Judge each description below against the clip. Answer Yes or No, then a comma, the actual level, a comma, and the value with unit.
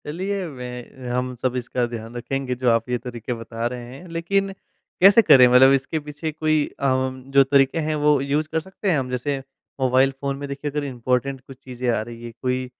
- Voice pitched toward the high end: No, low, 130 Hz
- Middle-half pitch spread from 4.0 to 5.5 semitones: No, average, 2.9 semitones